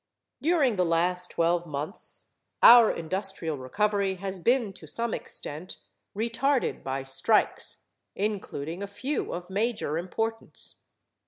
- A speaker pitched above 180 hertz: Yes, high, 190 Hz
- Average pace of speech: No, slow, 115 wpm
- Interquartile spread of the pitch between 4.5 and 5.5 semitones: Yes, average, 5.1 semitones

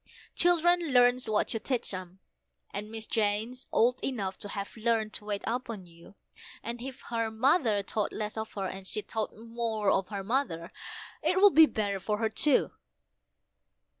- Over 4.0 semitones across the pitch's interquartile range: No, average, 3.4 semitones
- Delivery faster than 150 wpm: Yes, average, 170 wpm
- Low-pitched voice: No, high, 220 Hz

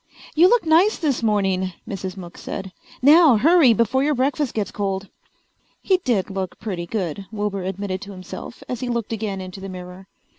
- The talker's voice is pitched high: Yes, high, 205 Hz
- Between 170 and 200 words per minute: Yes, average, 180 wpm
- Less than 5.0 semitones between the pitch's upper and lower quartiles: No, wide, 5.5 semitones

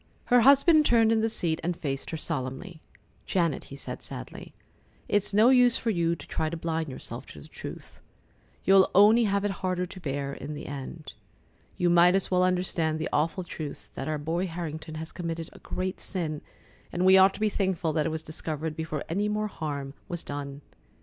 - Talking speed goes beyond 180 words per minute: Yes, average, 200 wpm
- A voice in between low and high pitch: Yes, medium, 170 Hz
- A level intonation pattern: No, average, 3.8 semitones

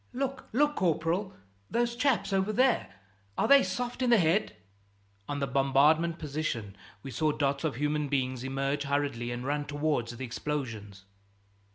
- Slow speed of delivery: No, average, 155 wpm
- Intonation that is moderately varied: No, wide, 6.3 semitones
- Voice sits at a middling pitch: Yes, medium, 150 Hz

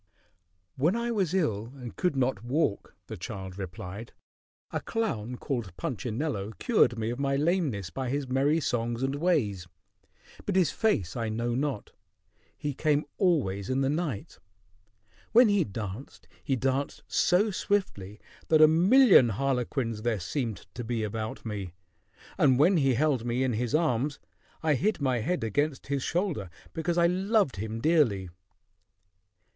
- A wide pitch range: Yes, wide, 6.3 semitones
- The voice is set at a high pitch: No, low, 130 Hz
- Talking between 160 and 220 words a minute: No, average, 150 wpm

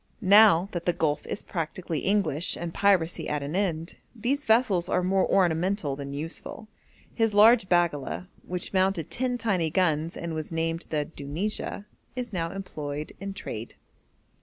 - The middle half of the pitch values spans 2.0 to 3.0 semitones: No, average, 3.9 semitones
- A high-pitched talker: No, medium, 175 Hz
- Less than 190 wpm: Yes, average, 155 wpm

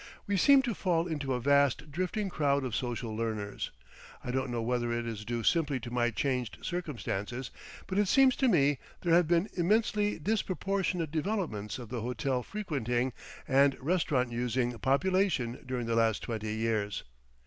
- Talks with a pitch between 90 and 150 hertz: Yes, low, 135 Hz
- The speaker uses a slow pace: No, average, 165 wpm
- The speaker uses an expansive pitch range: Yes, wide, 6.9 semitones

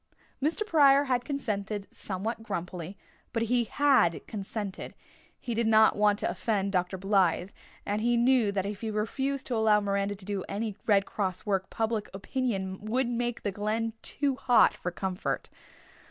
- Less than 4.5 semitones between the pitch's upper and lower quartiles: Yes, average, 3.3 semitones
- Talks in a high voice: Yes, high, 215 Hz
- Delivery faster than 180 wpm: No, average, 165 wpm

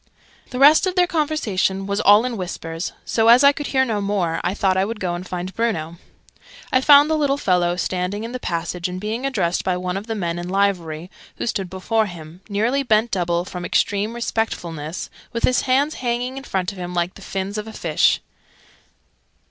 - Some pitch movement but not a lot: Yes, average, 5.0 semitones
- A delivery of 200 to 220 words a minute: Yes, fast, 205 wpm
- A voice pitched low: No, high, 200 Hz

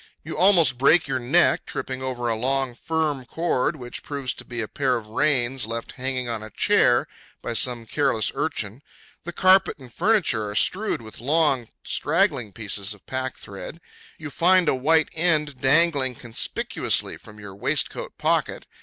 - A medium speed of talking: Yes, average, 165 wpm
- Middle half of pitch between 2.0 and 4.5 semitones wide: No, average, 5.0 semitones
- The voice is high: No, low, 130 Hz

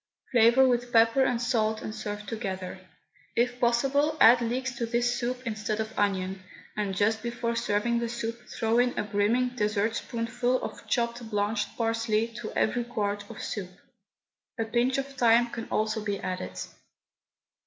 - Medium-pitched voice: No, high, 230 Hz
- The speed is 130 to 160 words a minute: Yes, average, 155 wpm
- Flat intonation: Yes, narrow, 2.2 semitones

